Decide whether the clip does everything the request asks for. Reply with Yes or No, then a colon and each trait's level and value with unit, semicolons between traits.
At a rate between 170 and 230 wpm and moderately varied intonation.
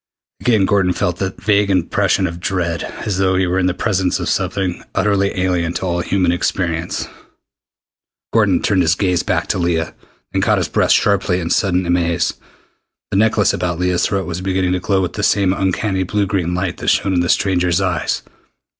No: average, 190 wpm; narrow, 1.7 semitones